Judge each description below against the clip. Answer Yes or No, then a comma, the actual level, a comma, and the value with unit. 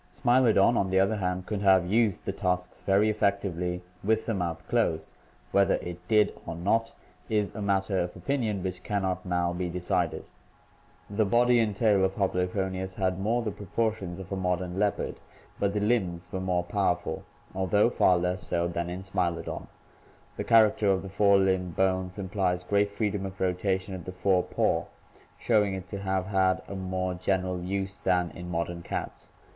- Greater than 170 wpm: Yes, average, 185 wpm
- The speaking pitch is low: Yes, very low, 95 Hz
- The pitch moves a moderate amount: No, narrow, 2.1 semitones